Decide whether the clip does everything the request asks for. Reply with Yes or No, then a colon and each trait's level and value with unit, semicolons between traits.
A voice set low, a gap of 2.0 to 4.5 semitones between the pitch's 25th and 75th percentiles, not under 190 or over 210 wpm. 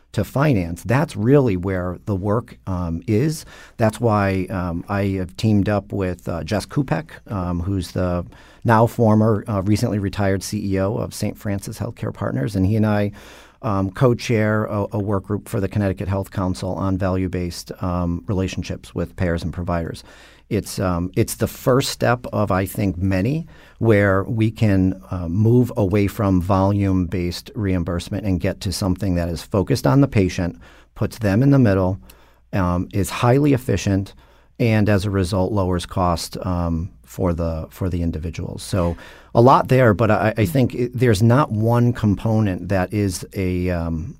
No: low, 100 Hz; average, 3.2 semitones; average, 170 wpm